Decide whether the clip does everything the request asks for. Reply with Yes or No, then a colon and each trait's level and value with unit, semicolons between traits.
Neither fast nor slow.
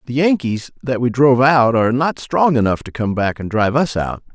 No: fast, 235 wpm